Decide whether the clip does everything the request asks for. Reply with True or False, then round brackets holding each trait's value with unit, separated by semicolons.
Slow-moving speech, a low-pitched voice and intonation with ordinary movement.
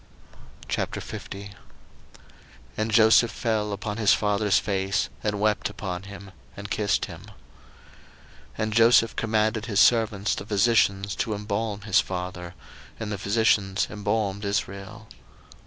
False (125 wpm; 105 Hz; 1.7 semitones)